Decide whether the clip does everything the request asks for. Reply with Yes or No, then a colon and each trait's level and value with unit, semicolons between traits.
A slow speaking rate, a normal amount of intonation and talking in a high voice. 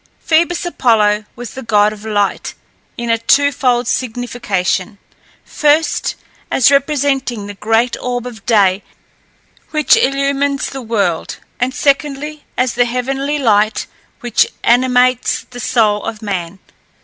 Yes: slow, 125 wpm; average, 4.3 semitones; high, 245 Hz